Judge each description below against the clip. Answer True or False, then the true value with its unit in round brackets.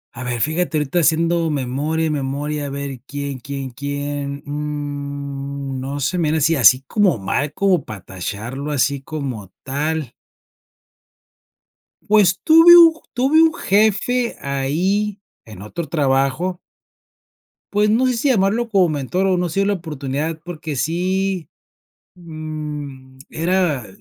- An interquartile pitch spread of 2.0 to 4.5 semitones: False (4.9 semitones)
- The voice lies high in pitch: False (150 Hz)